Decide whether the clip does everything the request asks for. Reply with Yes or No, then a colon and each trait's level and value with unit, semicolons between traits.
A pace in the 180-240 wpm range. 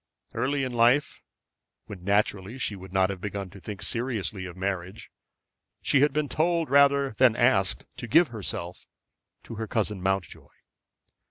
No: average, 155 wpm